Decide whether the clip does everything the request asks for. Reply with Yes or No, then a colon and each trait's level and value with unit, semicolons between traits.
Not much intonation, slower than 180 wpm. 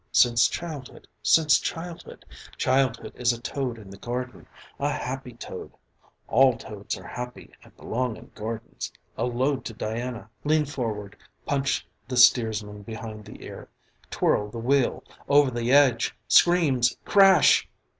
No: average, 3.3 semitones; average, 140 wpm